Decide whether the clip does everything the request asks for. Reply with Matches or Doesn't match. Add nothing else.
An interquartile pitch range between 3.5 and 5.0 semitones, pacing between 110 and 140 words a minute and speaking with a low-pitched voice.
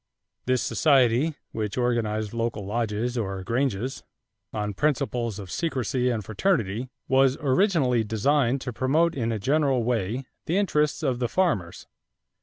Matches